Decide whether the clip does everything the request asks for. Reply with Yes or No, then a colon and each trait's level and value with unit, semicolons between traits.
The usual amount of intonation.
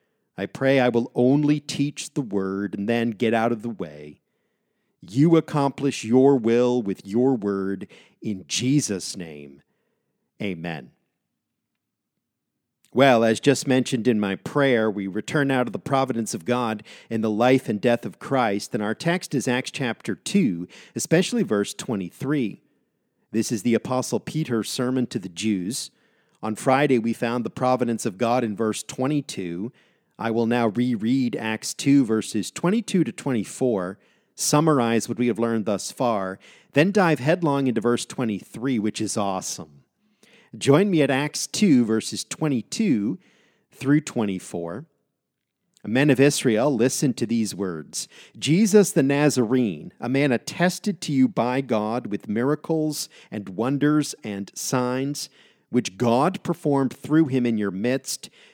Yes: average, 4.5 semitones